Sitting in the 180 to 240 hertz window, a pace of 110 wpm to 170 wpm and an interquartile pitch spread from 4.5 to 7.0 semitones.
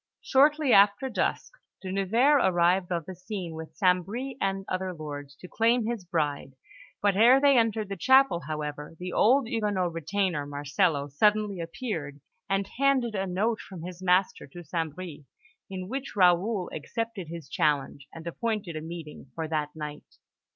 Yes: medium, 185 Hz; average, 165 wpm; average, 5.1 semitones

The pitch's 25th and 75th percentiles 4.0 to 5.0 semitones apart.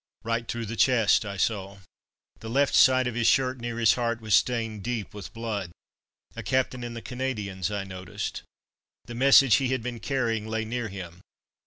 No: average, 2.9 semitones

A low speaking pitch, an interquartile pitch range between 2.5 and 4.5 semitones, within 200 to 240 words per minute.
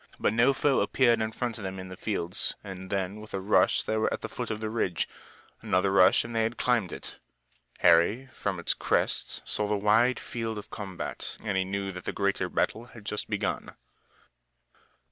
Yes: low, 105 Hz; average, 2.9 semitones; fast, 205 wpm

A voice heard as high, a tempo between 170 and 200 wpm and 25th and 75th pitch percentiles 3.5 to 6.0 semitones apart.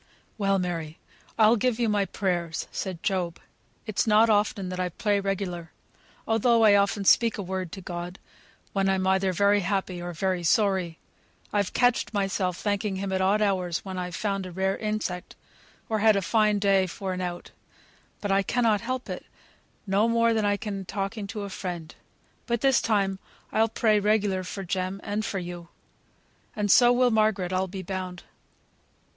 No: high, 195 Hz; average, 175 wpm; narrow, 2.5 semitones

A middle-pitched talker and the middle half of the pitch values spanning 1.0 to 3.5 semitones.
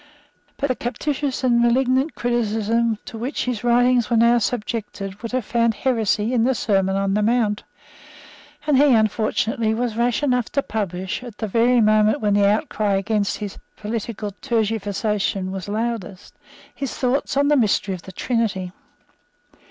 No: high, 225 Hz; average, 2.9 semitones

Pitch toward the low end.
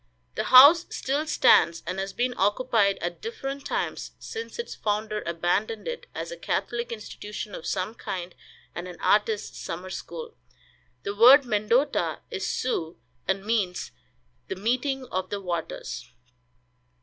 No: high, 215 Hz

